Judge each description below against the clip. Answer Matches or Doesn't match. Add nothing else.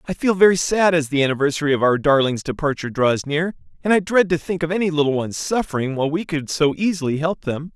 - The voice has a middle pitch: Matches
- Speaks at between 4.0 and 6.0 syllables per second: Doesn't match